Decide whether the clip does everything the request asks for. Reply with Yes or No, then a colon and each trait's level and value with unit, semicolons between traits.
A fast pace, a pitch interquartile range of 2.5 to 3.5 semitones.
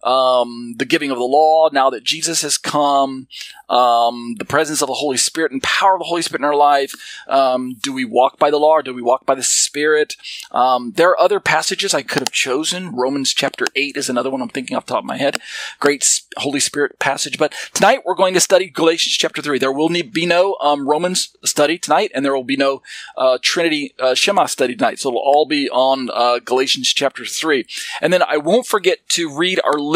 No: fast, 225 wpm; average, 4.0 semitones